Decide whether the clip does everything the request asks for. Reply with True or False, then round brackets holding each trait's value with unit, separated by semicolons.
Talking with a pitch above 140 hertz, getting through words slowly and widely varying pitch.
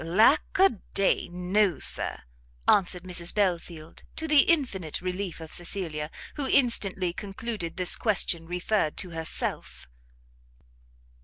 False (185 Hz; 120 wpm; 3.8 semitones)